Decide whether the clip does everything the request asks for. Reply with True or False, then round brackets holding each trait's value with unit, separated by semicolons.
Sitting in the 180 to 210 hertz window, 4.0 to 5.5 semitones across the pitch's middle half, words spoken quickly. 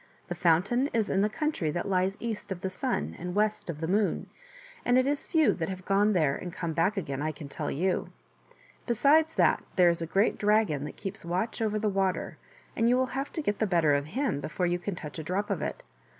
True (190 Hz; 4.4 semitones; 235 wpm)